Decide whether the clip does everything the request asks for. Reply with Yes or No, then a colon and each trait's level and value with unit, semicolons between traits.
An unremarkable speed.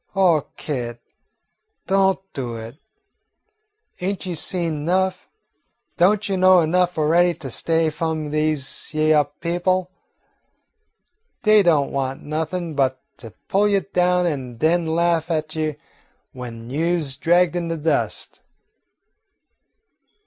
No: slow, 125 wpm